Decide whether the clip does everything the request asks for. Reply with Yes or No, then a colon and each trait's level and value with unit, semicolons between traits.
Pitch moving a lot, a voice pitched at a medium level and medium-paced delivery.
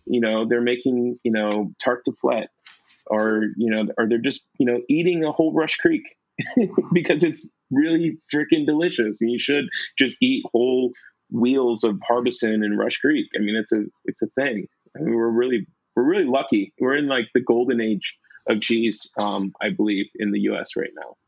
No: wide, 5.9 semitones; low, 120 Hz; average, 195 wpm